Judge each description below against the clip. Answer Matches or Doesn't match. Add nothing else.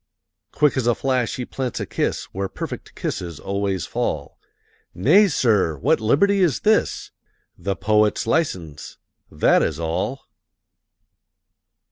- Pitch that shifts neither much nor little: Doesn't match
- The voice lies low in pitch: Matches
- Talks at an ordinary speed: Doesn't match